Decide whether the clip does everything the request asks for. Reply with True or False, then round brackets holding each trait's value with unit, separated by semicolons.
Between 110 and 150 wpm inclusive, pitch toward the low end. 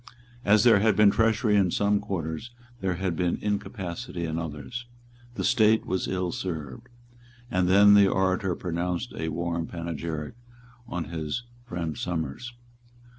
True (140 wpm; 90 Hz)